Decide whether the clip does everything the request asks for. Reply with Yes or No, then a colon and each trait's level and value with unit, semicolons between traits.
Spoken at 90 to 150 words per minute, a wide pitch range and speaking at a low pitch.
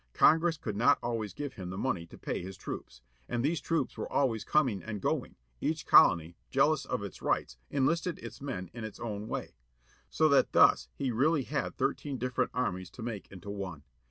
No: average, 195 wpm; wide, 6.6 semitones; low, 115 Hz